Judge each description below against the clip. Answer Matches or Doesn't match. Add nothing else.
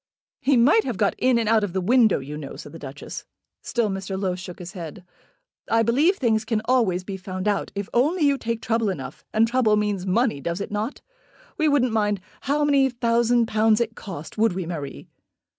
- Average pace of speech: Doesn't match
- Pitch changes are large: Doesn't match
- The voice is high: Matches